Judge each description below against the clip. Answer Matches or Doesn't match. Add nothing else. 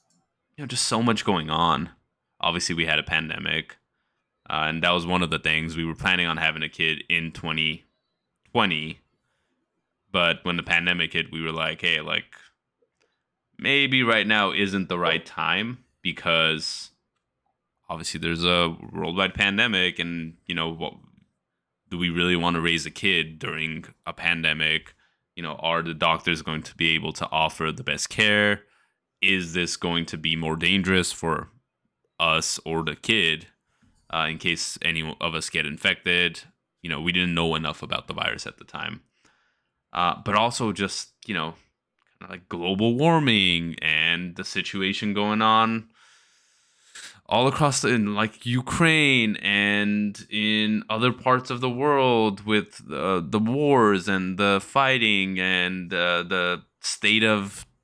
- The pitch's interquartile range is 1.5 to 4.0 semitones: Doesn't match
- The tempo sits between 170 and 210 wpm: Doesn't match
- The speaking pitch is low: Matches